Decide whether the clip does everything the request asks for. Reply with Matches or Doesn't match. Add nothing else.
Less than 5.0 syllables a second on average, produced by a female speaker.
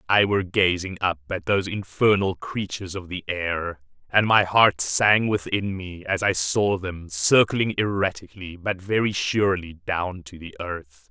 Doesn't match